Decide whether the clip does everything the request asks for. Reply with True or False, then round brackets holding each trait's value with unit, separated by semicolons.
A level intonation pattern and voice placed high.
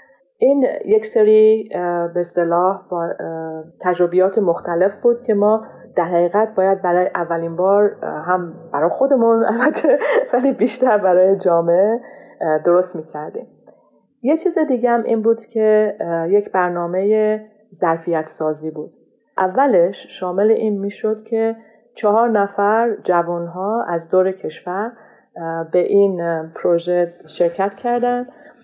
False (4.7 semitones; 195 Hz)